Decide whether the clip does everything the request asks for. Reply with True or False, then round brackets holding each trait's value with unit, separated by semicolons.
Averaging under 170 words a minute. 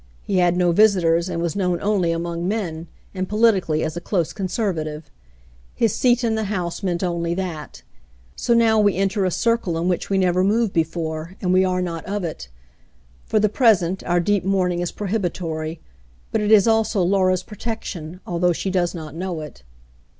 False (185 wpm)